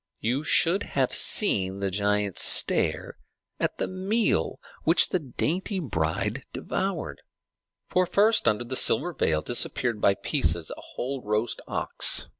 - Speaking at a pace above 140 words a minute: No, slow, 135 wpm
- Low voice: Yes, low, 120 Hz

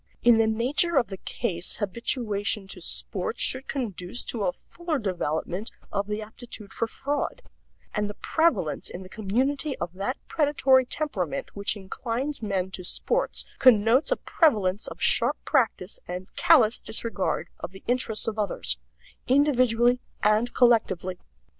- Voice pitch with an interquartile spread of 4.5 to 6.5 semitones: Yes, average, 5.0 semitones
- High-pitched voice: Yes, high, 225 Hz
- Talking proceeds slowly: No, average, 145 wpm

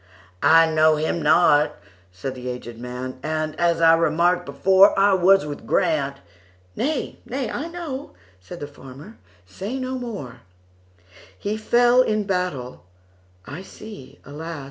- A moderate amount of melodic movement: No, wide, 8.0 semitones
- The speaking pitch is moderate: Yes, medium, 155 Hz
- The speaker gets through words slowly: Yes, slow, 115 wpm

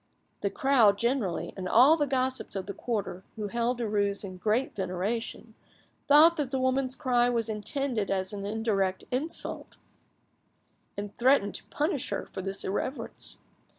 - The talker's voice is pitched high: Yes, high, 230 Hz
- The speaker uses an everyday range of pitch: Yes, average, 4.6 semitones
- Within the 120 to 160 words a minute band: Yes, average, 150 wpm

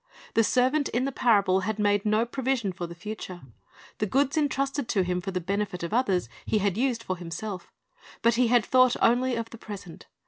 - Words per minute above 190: Yes, fast, 205 wpm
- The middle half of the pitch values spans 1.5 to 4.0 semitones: No, average, 4.8 semitones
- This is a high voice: Yes, high, 215 Hz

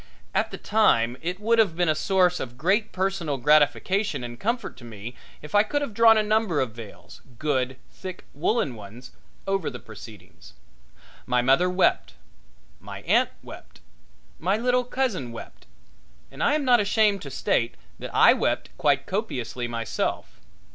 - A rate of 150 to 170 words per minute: Yes, average, 160 wpm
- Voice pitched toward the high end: No, medium, 170 Hz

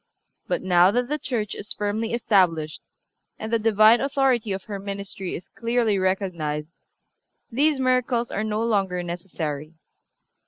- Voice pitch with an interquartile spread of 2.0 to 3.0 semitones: No, average, 4.2 semitones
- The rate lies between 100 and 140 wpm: Yes, slow, 135 wpm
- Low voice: No, high, 210 Hz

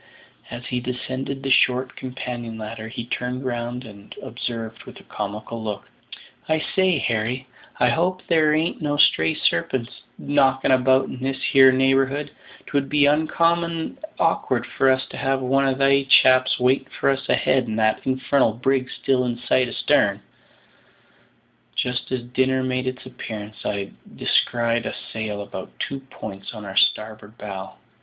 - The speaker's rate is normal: Yes, average, 155 wpm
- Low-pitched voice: Yes, low, 130 Hz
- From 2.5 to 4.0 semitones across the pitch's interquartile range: Yes, average, 2.8 semitones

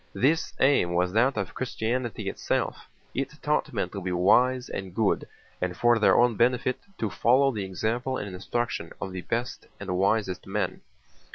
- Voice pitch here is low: Yes, low, 110 Hz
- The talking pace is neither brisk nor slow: Yes, average, 170 wpm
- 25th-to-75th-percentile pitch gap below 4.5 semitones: No, average, 4.8 semitones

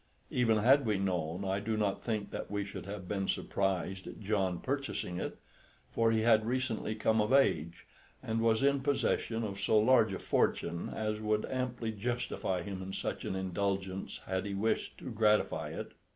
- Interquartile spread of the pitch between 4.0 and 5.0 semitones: No, average, 2.9 semitones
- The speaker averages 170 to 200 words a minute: Yes, average, 180 wpm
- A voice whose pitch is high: No, low, 105 Hz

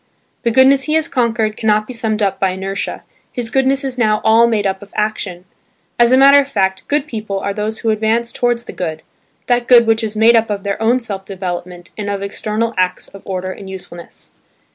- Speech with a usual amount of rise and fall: Yes, average, 3.4 semitones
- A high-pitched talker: Yes, high, 215 Hz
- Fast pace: Yes, fast, 210 wpm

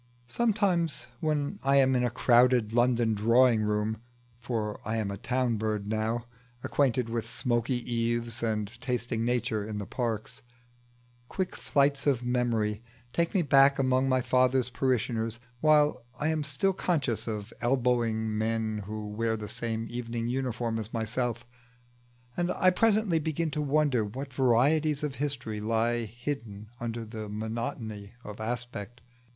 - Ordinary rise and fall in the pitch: Yes, average, 3.4 semitones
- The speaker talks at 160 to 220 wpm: No, average, 145 wpm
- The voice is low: Yes, low, 120 Hz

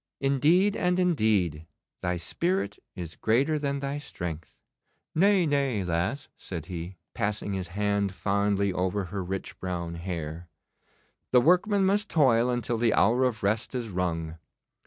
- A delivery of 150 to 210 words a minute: No, average, 140 wpm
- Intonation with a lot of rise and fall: Yes, wide, 7.7 semitones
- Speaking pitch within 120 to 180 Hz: No, low, 105 Hz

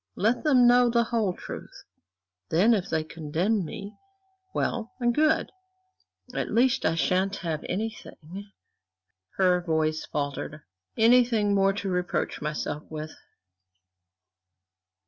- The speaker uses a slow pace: Yes, slow, 115 wpm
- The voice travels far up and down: Yes, wide, 6.3 semitones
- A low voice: No, high, 195 Hz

